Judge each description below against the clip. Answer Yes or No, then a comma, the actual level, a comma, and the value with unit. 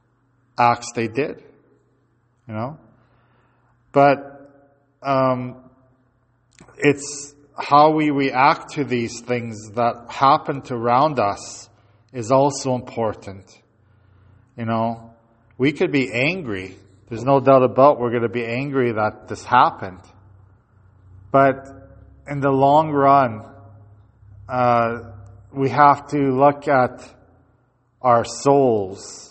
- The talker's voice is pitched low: Yes, low, 120 Hz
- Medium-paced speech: No, slow, 105 wpm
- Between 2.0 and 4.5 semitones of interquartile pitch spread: Yes, average, 3.4 semitones